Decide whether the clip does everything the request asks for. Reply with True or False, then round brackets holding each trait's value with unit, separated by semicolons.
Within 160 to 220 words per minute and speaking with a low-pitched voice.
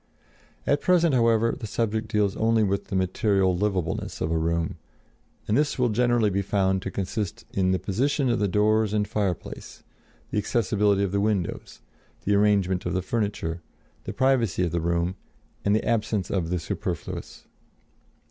True (165 wpm; 100 Hz)